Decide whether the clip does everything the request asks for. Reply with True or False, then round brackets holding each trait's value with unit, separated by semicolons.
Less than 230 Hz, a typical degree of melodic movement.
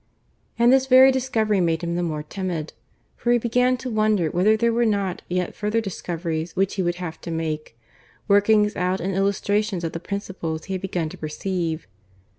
True (190 Hz; 4.3 semitones)